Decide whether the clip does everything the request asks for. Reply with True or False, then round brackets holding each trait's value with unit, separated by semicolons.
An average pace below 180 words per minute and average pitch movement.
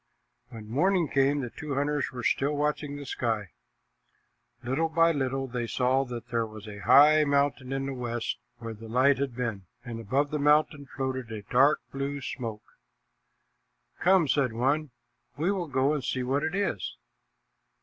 True (170 wpm; 3.5 semitones)